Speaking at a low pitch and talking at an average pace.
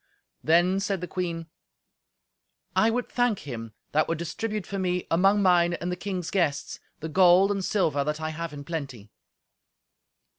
No: medium, 175 Hz; average, 160 wpm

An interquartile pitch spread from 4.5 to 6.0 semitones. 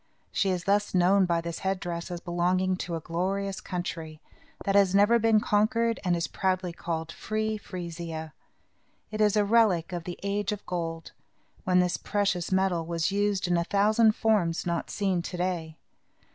No: average, 3.0 semitones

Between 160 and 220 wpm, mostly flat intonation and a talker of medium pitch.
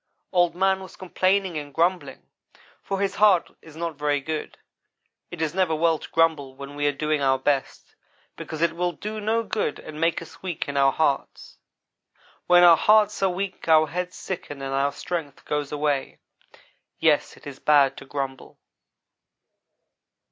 No: average, 170 wpm; average, 3.9 semitones; medium, 160 Hz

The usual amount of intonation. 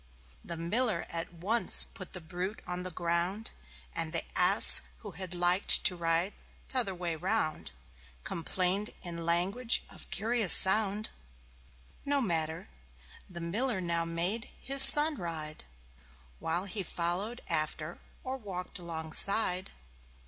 Yes: average, 3.9 semitones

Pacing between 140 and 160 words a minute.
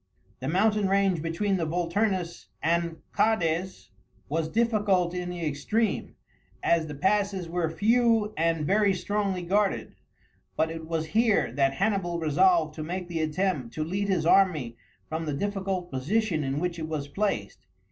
Yes: average, 155 wpm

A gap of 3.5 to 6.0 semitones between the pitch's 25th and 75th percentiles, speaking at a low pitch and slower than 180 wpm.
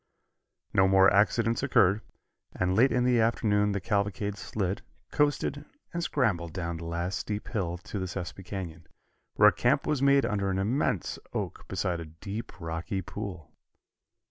Yes: average, 3.9 semitones; low, 100 Hz; average, 160 wpm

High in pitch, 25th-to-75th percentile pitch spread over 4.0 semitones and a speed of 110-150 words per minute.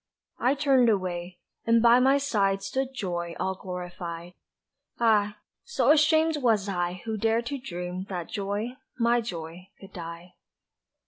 Yes: high, 200 Hz; average, 5.2 semitones; average, 140 wpm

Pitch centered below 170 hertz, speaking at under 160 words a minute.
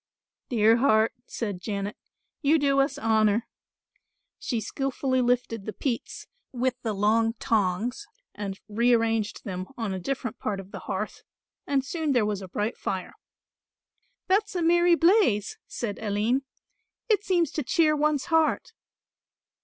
No: high, 235 Hz; average, 140 wpm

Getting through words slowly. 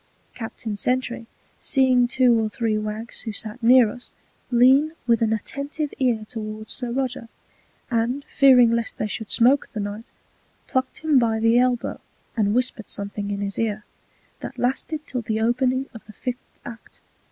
No: average, 165 wpm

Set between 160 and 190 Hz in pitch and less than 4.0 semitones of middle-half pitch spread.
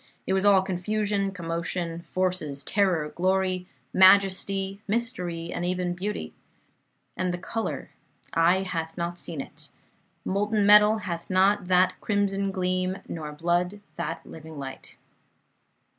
Yes: medium, 185 Hz; narrow, 2.4 semitones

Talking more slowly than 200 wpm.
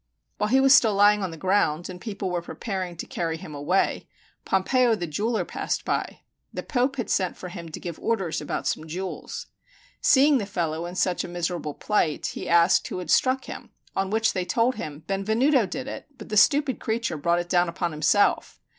No: fast, 205 wpm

